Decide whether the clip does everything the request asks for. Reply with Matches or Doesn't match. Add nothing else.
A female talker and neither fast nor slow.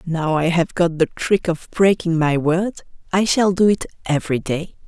Matches